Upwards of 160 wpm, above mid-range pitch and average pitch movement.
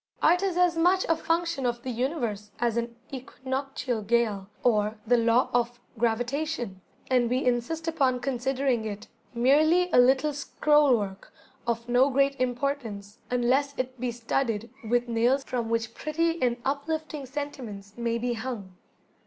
No: average, 150 wpm; very high, 250 Hz; average, 3.2 semitones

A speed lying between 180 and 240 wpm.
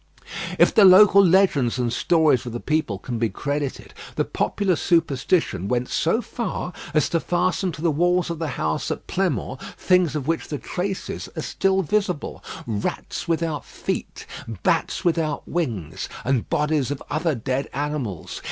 No: average, 160 wpm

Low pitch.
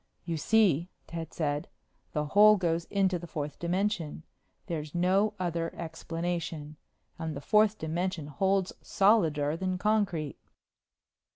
No: medium, 170 Hz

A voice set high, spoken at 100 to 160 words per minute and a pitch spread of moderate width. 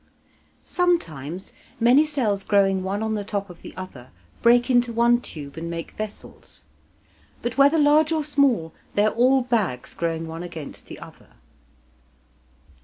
No: high, 215 Hz; average, 150 wpm; wide, 7.0 semitones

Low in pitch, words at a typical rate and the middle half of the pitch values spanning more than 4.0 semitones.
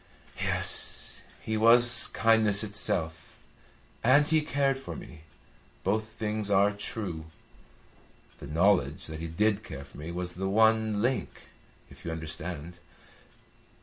No: low, 105 Hz; slow, 125 wpm; average, 4.8 semitones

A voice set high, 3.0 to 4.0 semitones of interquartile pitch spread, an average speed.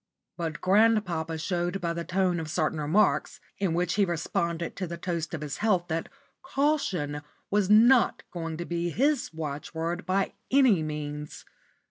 No: medium, 175 Hz; average, 3.4 semitones; average, 155 wpm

